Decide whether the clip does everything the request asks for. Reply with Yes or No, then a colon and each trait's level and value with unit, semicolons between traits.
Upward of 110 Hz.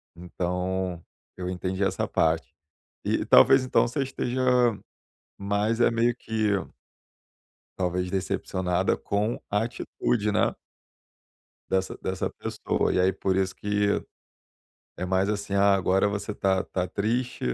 No: low, 100 Hz